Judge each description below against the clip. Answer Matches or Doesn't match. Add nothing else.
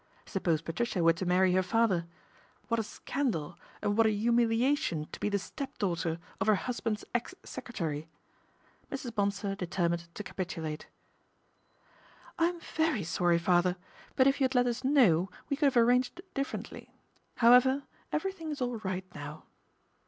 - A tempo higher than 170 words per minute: Doesn't match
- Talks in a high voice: Matches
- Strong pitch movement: Matches